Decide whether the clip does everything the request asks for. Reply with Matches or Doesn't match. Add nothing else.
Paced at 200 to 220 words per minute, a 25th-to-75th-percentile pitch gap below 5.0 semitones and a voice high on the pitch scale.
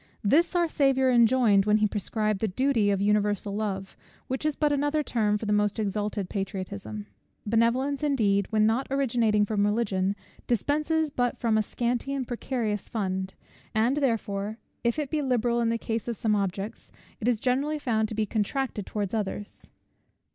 Doesn't match